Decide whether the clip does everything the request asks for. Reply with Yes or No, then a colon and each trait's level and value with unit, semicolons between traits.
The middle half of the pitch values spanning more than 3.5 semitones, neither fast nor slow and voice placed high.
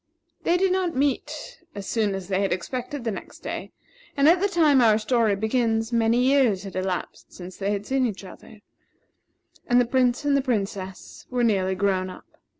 Yes: average, 5.1 semitones; average, 190 wpm; high, 225 Hz